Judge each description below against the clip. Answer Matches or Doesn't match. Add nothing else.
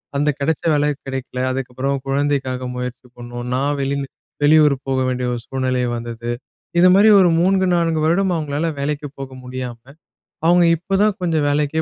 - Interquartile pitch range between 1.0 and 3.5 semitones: Doesn't match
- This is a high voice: Doesn't match